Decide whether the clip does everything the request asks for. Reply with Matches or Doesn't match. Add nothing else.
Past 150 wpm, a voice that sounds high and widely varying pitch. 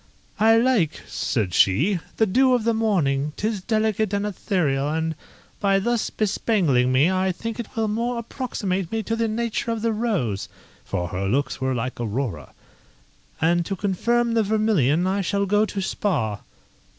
Matches